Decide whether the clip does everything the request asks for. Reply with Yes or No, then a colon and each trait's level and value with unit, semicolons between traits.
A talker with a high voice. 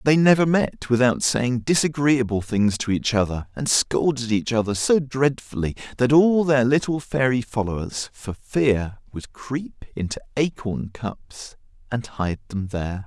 No: low, 125 Hz